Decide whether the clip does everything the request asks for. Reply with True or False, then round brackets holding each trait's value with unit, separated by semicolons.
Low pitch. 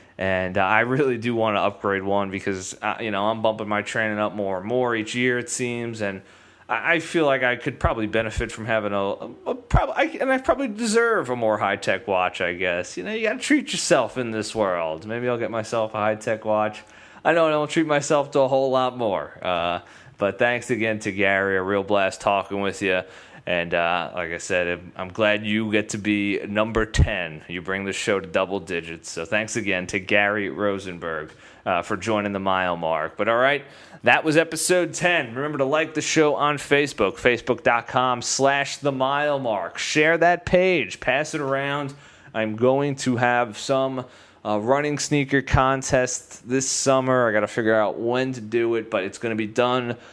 True (115 Hz)